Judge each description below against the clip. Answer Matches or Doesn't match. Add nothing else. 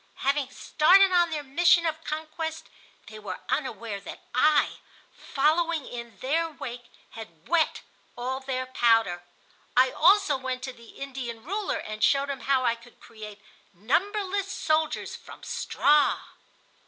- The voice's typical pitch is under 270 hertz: Doesn't match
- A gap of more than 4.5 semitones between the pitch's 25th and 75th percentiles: Matches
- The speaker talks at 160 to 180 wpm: Doesn't match